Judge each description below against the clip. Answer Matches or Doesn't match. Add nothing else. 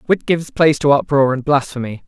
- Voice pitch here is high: Doesn't match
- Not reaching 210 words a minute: Matches